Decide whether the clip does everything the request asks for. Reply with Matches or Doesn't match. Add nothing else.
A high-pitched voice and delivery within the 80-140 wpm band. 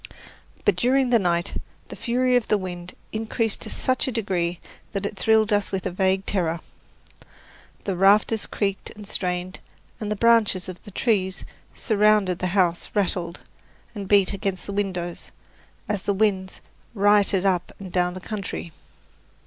Doesn't match